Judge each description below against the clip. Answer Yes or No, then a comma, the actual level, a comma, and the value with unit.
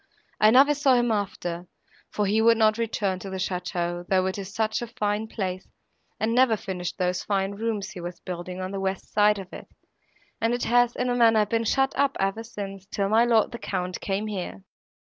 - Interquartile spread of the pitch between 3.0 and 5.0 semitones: Yes, average, 3.5 semitones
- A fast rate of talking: Yes, fast, 210 wpm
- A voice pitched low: No, high, 205 Hz